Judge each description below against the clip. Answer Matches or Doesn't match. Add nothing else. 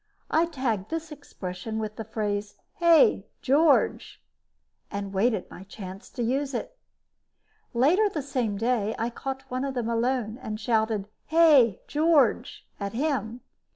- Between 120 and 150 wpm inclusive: Matches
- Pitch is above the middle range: Matches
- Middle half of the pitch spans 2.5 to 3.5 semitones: Doesn't match